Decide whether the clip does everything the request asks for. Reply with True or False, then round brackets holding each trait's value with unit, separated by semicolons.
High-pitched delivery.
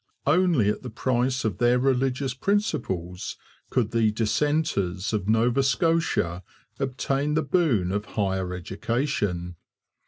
False (120 Hz)